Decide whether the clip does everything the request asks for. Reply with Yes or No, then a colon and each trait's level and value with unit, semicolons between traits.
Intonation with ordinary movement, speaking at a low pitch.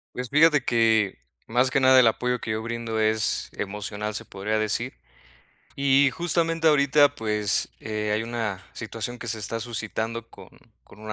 Yes: average, 3.3 semitones; low, 115 Hz